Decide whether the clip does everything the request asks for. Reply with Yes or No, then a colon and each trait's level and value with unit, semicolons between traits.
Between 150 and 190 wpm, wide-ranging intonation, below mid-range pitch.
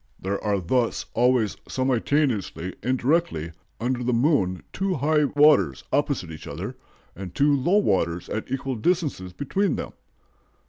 No: average, 140 wpm; wide, 7.4 semitones; low, 125 Hz